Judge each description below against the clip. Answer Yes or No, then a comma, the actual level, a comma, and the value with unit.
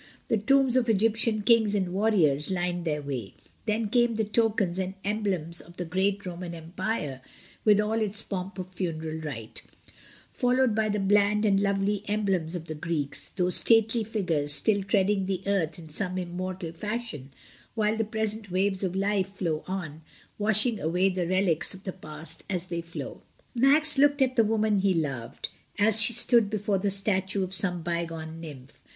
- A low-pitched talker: No, high, 195 Hz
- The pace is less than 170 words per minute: No, average, 175 wpm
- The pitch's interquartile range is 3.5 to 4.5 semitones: Yes, average, 3.9 semitones